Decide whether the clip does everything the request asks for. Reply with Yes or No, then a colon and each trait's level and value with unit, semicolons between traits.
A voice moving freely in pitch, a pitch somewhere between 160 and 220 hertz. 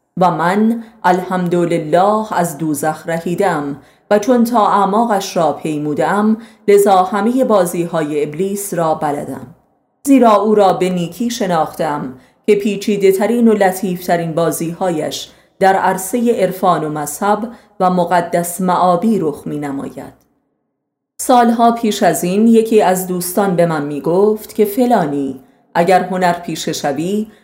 No: average, 3.9 semitones; medium, 185 Hz